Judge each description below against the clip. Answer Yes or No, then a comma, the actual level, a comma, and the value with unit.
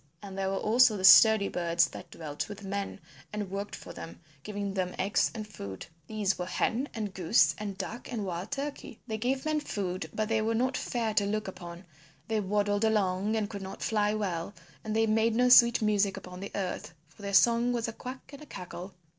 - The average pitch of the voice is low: No, high, 205 Hz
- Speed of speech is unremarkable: No, fast, 215 wpm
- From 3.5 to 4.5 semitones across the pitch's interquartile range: No, average, 2.7 semitones